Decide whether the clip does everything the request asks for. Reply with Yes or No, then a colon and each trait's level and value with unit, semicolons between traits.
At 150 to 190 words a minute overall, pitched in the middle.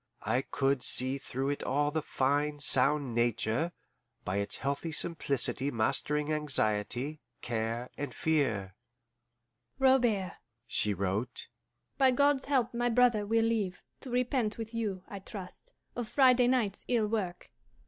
No: slow, 135 wpm; medium, 155 Hz